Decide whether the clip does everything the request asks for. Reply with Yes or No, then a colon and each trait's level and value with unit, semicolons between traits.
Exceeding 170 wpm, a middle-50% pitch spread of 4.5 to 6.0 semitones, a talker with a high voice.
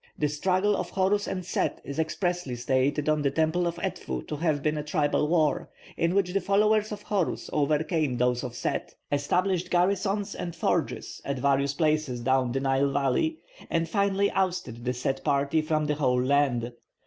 No: average, 180 wpm; average, 4.9 semitones; medium, 155 Hz